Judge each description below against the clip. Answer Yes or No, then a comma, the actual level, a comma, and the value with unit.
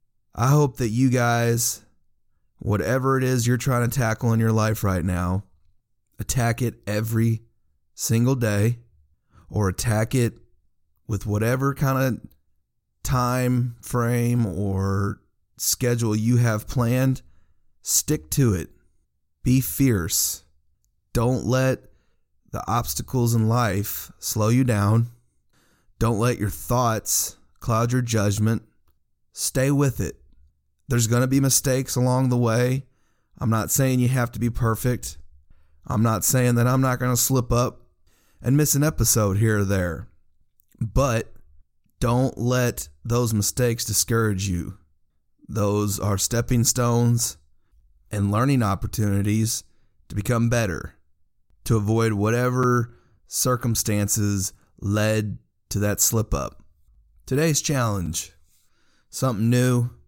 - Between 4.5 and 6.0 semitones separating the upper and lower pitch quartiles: No, average, 3.7 semitones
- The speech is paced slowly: Yes, slow, 125 wpm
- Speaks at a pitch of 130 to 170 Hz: No, low, 115 Hz